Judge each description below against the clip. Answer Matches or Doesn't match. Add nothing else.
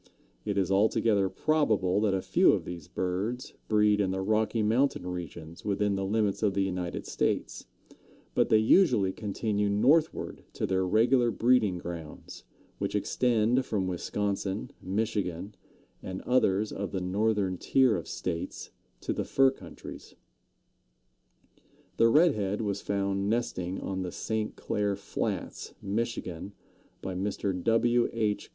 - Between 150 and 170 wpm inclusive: Doesn't match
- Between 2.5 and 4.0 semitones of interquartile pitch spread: Matches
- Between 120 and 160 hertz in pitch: Doesn't match